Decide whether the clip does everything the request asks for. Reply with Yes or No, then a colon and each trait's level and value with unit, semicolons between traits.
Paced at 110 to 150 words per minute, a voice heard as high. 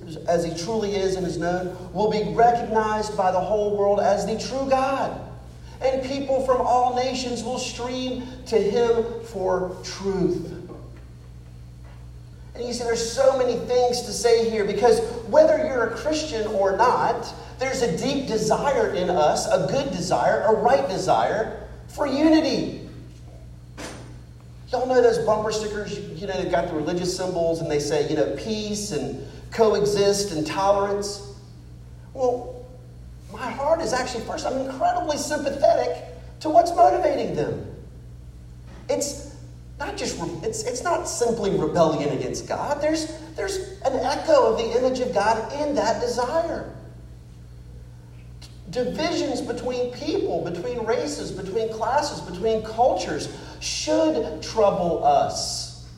Yes: average, 140 wpm; high, 210 Hz